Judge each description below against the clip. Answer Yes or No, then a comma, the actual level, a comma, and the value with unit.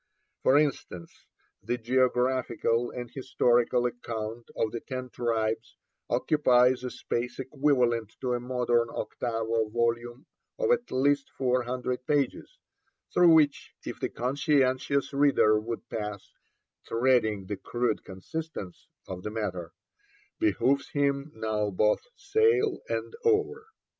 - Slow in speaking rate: Yes, slow, 120 wpm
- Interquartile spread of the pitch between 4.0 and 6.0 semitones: No, average, 3.5 semitones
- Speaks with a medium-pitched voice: No, low, 125 Hz